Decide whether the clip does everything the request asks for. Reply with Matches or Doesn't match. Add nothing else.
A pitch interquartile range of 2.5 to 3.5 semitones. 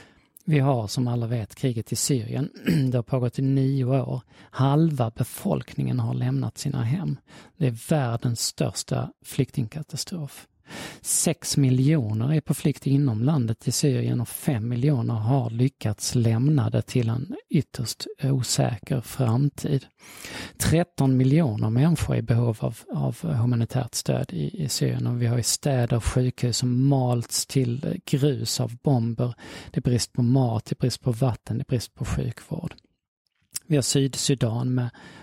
Matches